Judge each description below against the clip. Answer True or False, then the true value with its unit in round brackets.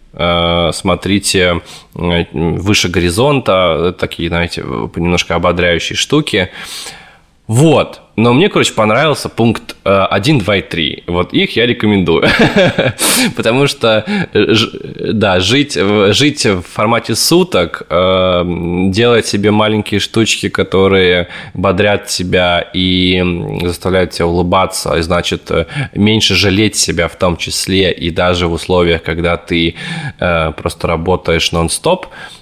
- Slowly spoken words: True (105 wpm)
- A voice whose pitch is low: True (90 Hz)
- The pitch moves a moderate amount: True (3.7 semitones)